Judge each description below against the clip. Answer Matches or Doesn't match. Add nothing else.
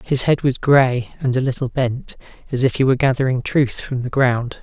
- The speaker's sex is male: Matches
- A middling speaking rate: Doesn't match